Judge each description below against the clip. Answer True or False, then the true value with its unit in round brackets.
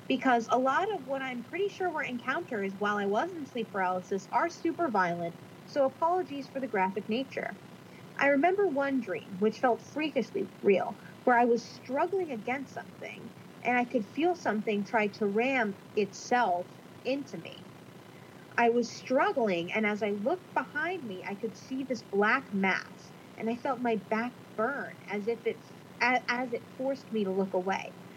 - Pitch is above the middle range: True (235 Hz)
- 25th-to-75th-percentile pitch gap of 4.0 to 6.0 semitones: True (4.7 semitones)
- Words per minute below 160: False (175 wpm)